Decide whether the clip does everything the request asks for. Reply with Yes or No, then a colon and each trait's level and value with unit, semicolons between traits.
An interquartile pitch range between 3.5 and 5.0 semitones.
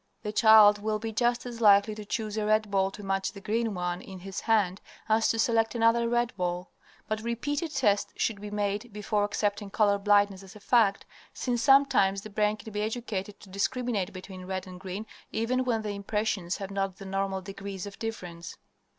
No: narrow, 2.4 semitones